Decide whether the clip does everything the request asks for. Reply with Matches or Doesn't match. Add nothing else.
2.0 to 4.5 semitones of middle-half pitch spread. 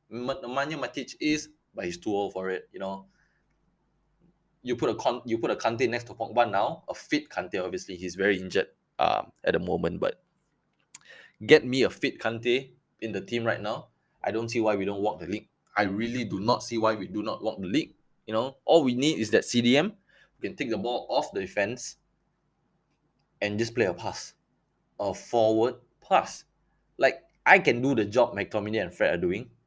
Doesn't match